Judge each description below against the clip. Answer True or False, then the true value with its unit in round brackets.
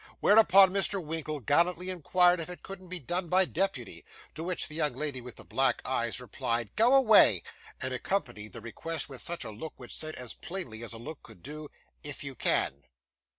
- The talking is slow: False (195 wpm)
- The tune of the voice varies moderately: False (6.7 semitones)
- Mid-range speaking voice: True (155 Hz)